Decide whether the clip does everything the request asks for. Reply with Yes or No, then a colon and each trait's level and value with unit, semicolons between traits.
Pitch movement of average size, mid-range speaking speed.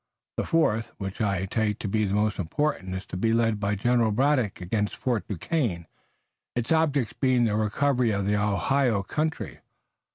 Yes: average, 4.0 semitones; average, 170 wpm